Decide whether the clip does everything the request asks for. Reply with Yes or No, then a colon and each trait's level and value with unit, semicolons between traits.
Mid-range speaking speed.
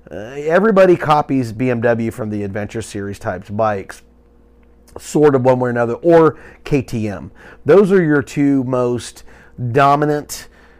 No: slow, 130 wpm